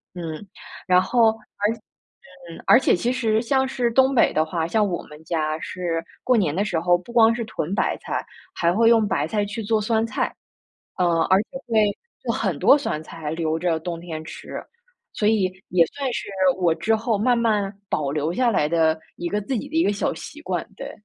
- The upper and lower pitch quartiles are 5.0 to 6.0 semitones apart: Yes, wide, 5.5 semitones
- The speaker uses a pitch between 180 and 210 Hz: Yes, high, 200 Hz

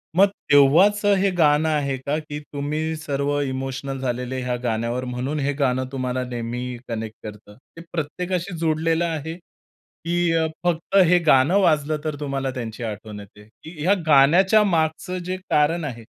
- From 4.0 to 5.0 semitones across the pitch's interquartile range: Yes, average, 4.4 semitones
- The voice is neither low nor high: Yes, medium, 145 Hz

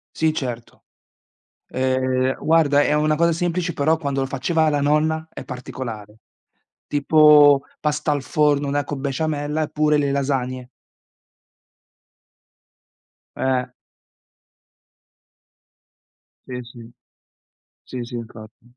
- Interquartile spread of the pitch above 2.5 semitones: Yes, average, 2.9 semitones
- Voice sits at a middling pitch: Yes, medium, 145 Hz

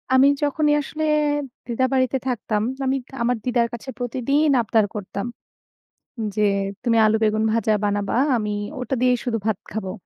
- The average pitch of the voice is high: Yes, high, 235 Hz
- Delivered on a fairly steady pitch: No, average, 3.1 semitones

